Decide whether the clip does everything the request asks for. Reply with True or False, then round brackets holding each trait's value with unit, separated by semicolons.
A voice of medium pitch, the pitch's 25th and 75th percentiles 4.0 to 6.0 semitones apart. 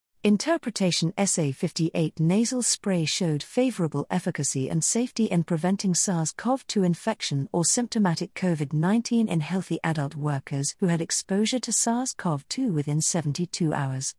True (175 Hz; 5.2 semitones)